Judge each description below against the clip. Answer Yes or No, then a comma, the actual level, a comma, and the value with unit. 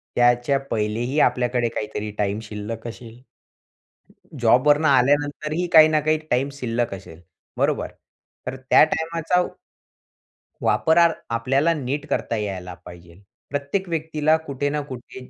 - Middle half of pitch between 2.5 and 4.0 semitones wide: No, average, 4.9 semitones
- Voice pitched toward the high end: No, low, 130 Hz